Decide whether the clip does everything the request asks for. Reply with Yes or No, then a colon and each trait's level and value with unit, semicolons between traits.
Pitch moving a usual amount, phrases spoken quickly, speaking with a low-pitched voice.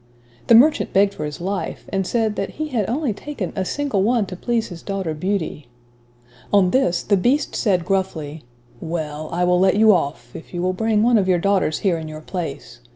No: average, 4.3 semitones; fast, 210 wpm; high, 190 Hz